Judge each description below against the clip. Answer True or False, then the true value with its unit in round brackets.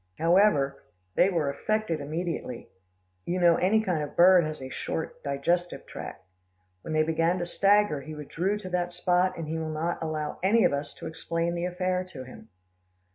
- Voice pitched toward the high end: False (170 Hz)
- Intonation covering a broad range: False (2.8 semitones)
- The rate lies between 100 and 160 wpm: False (185 wpm)